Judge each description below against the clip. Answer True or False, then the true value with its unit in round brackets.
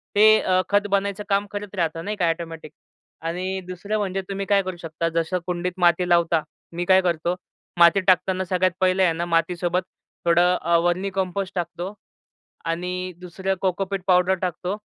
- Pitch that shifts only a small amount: True (1.9 semitones)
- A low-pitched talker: False (180 Hz)